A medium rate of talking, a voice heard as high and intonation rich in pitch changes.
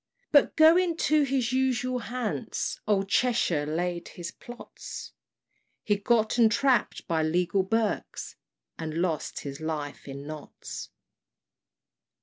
No: slow, 115 wpm; high, 210 Hz; wide, 7.6 semitones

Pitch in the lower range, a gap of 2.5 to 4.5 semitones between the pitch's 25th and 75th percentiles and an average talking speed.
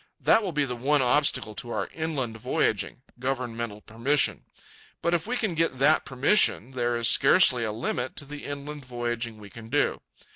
Yes: low, 130 Hz; average, 3.9 semitones; average, 175 wpm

